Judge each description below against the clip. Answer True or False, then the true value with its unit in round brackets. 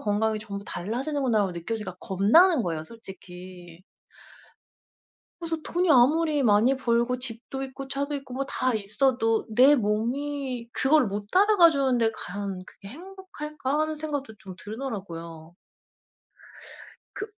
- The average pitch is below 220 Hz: False (240 Hz)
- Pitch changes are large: True (5.7 semitones)